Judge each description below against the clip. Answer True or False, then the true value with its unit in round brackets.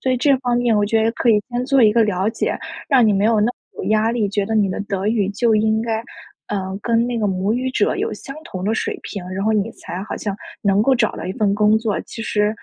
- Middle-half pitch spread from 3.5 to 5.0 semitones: False (2.4 semitones)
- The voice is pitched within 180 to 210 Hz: False (220 Hz)